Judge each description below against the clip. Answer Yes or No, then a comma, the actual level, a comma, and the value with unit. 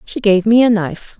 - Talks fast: Yes, fast, 250 wpm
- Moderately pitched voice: No, high, 205 Hz